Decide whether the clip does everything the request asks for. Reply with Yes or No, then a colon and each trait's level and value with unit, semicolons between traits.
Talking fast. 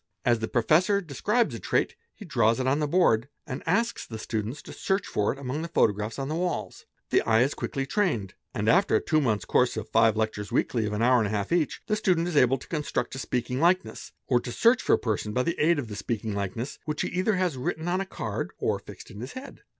Yes: fast, 245 wpm